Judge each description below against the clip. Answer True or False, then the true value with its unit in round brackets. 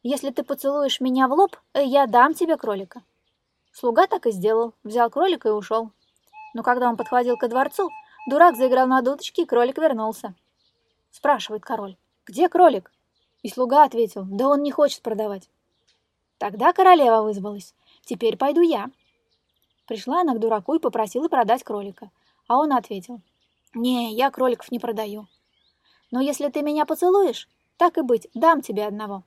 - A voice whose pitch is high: True (255 Hz)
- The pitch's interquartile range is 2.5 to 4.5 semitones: False (5.0 semitones)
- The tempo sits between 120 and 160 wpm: True (155 wpm)